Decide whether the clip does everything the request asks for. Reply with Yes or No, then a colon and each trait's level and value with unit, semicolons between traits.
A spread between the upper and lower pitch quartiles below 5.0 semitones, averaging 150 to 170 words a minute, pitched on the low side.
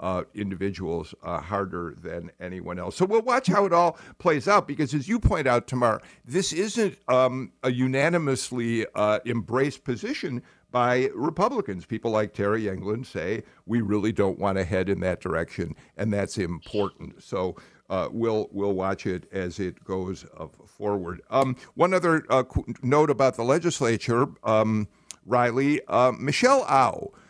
No: wide, 5.5 semitones; average, 155 wpm; low, 115 Hz